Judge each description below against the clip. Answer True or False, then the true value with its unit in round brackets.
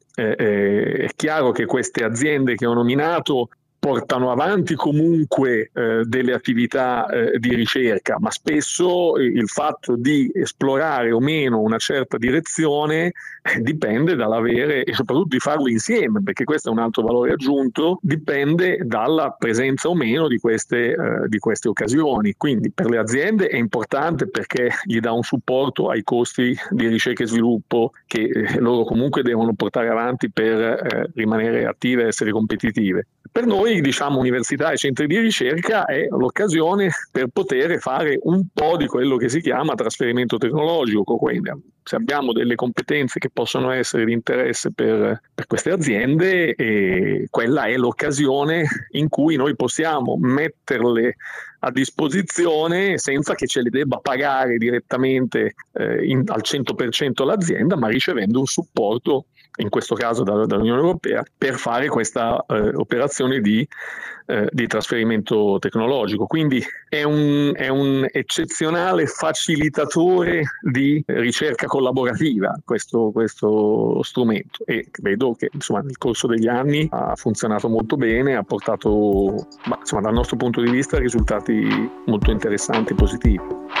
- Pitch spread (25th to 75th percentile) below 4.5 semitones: False (4.8 semitones)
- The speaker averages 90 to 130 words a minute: False (145 wpm)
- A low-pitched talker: True (130 Hz)